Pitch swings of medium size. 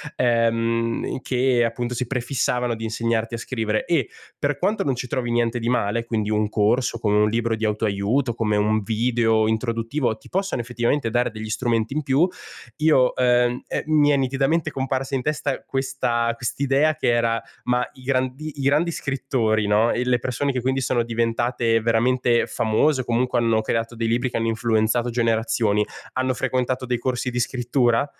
No: narrow, 2.3 semitones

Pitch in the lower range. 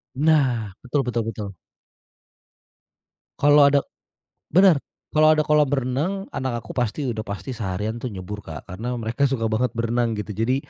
Yes: low, 120 Hz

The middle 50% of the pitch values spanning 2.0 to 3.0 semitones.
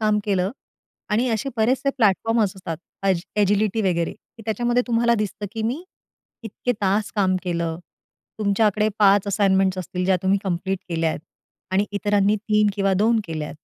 Yes: narrow, 2.6 semitones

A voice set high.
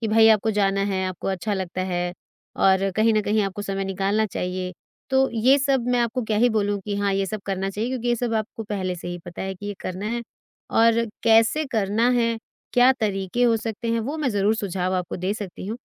Yes: high, 210 Hz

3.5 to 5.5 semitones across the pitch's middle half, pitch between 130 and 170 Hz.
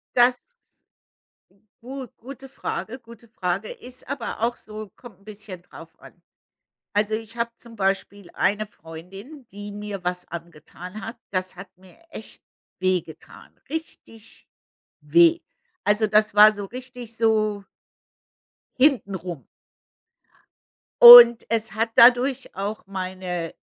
No: average, 3.8 semitones; high, 215 Hz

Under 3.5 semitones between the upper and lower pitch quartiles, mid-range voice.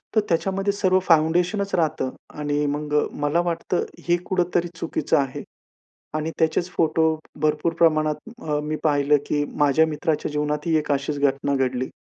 Yes: average, 2.7 semitones; medium, 155 Hz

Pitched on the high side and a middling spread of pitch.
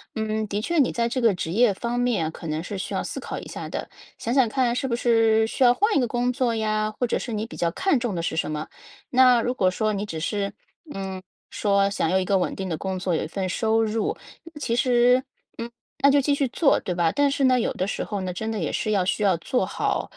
Yes: high, 220 Hz; average, 4.4 semitones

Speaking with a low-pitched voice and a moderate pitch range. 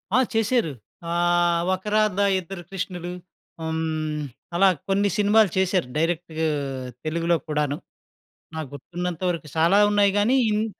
No: medium, 175 Hz; average, 3.8 semitones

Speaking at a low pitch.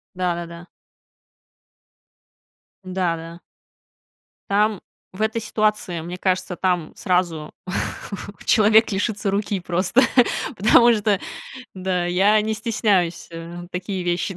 No: medium, 185 Hz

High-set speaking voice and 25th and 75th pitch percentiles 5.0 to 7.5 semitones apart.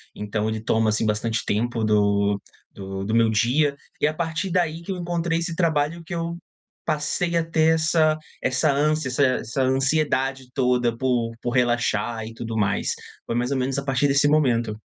No: low, 130 Hz; wide, 5.5 semitones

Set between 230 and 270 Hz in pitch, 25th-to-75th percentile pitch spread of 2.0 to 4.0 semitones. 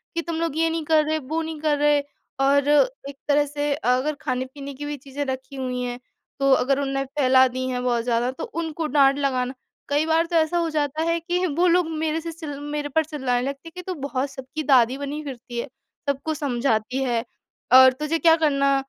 No: very high, 285 Hz; average, 3.3 semitones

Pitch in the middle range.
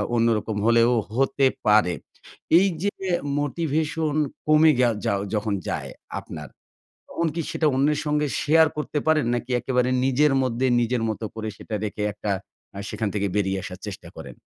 No: low, 125 Hz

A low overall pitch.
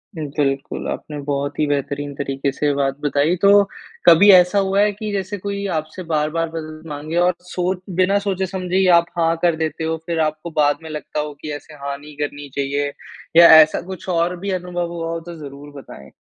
No: medium, 160 Hz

